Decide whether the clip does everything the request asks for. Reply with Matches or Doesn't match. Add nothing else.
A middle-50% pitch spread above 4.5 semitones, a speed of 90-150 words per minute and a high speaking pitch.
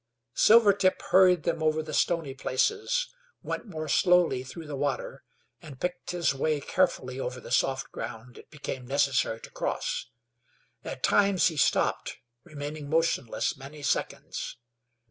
Doesn't match